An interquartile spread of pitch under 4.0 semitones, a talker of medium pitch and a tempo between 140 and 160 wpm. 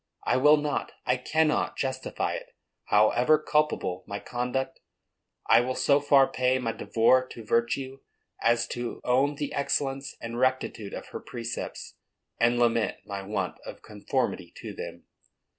No: average, 2.8 semitones; low, 125 Hz; average, 145 wpm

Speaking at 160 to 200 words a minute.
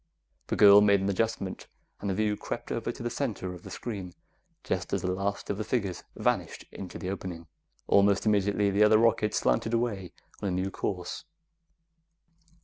Yes: average, 180 wpm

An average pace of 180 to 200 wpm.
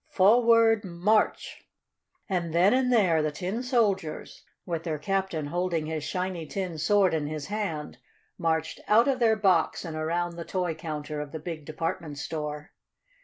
No: average, 160 wpm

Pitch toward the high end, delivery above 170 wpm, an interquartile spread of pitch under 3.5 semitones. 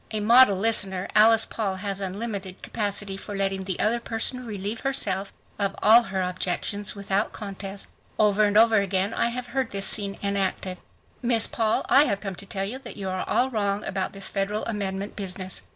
Yes: high, 200 Hz; average, 185 wpm; narrow, 2.4 semitones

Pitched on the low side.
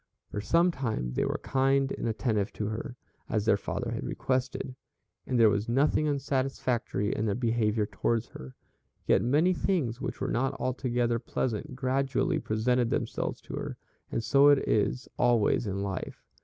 Yes: low, 120 Hz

